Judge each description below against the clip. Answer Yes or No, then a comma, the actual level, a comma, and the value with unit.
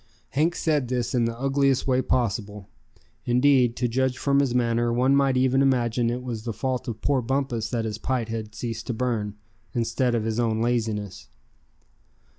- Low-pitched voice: Yes, low, 120 Hz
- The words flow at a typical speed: Yes, average, 180 wpm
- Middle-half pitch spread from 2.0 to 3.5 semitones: Yes, narrow, 2.5 semitones